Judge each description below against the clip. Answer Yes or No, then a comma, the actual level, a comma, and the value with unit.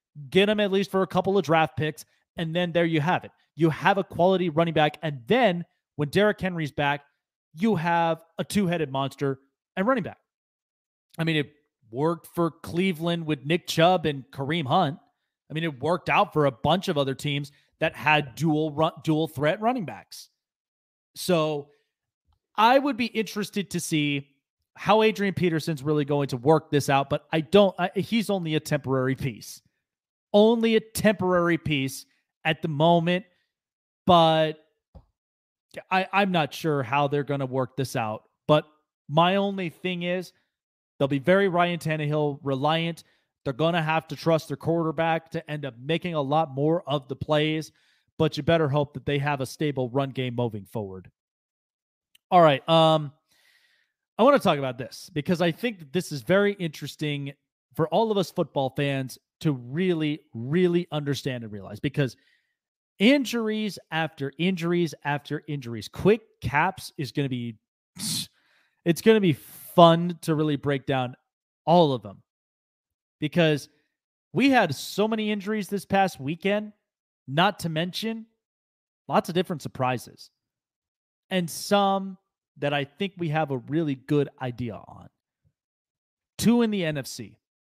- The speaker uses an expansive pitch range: No, average, 4.2 semitones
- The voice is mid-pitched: Yes, medium, 160 Hz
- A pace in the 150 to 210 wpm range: Yes, average, 165 wpm